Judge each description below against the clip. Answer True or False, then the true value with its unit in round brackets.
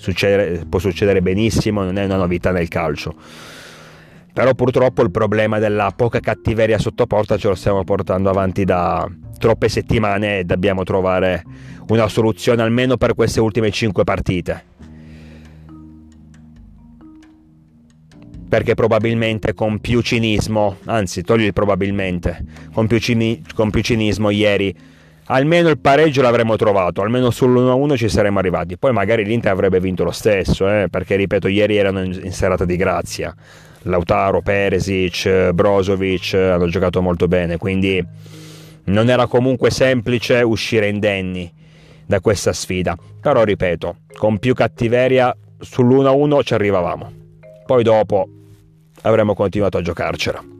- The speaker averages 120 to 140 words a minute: True (130 wpm)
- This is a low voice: True (105 Hz)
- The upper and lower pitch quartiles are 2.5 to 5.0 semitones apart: True (4.1 semitones)